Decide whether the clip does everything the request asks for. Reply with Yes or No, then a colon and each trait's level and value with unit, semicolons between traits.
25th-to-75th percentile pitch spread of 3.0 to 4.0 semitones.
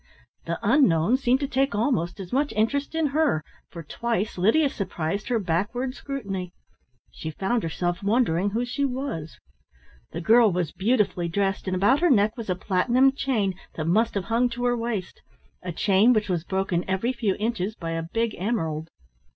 No: average, 5.3 semitones